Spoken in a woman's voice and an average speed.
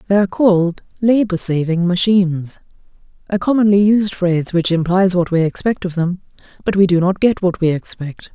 Yes: female; average, 175 wpm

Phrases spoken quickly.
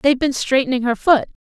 Yes: fast, 210 wpm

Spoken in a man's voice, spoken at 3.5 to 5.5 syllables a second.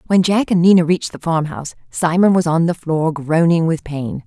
No: female; 5.3 syllables/s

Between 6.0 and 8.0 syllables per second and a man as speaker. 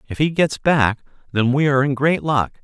No: 5.2 syllables/s; male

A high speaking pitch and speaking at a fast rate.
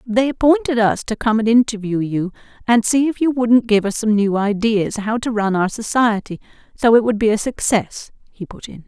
Yes: high, 220 Hz; fast, 215 wpm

